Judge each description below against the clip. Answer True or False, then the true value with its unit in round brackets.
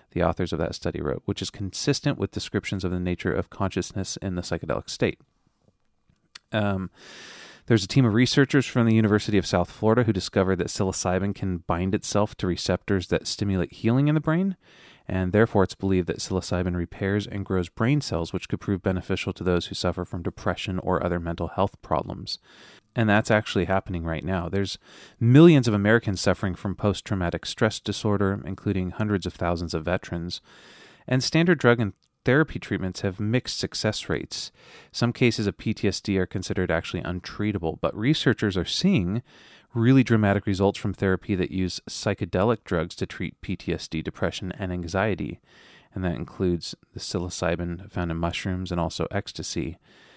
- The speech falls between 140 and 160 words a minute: False (170 wpm)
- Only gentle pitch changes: False (3.3 semitones)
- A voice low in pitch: True (95 Hz)